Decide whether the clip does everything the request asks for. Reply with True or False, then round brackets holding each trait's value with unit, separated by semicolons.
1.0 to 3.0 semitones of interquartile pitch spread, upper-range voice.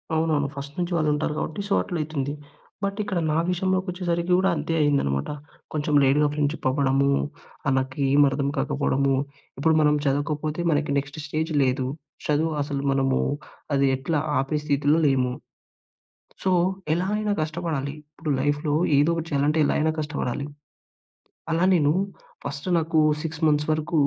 False (2.5 semitones; 150 Hz)